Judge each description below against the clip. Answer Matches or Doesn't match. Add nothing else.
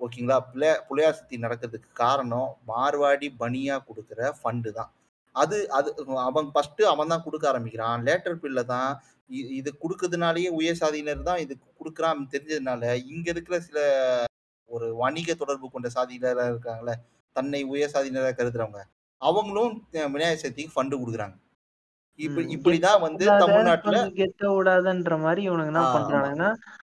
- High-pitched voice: Doesn't match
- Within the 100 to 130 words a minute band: Matches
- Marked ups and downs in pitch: Doesn't match